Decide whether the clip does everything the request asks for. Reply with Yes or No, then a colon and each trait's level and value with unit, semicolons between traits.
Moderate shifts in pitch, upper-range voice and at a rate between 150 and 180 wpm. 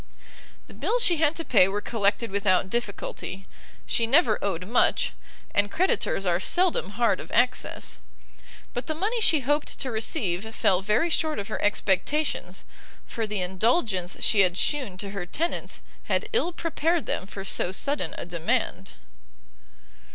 No: wide, 7.7 semitones; high, 220 Hz; average, 155 wpm